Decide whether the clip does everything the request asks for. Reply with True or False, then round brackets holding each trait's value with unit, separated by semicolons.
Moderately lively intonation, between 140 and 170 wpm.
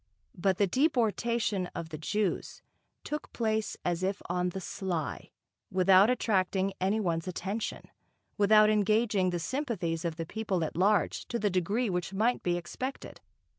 True (3.5 semitones; 150 wpm)